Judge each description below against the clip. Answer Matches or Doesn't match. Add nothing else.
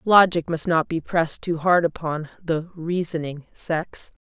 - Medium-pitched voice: Matches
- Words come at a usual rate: Matches